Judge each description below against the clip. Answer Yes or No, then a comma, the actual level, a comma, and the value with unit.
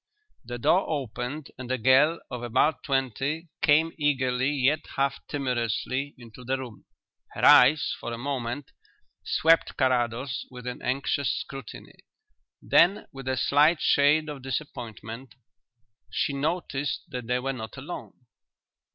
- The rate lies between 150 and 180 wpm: No, slow, 135 wpm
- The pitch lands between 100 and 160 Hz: Yes, low, 135 Hz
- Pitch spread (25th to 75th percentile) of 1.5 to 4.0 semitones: Yes, average, 2.8 semitones